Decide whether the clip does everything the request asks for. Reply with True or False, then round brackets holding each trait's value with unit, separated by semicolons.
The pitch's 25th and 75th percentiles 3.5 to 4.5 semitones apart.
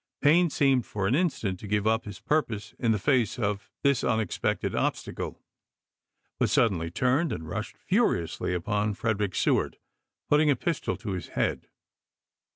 False (5.6 semitones)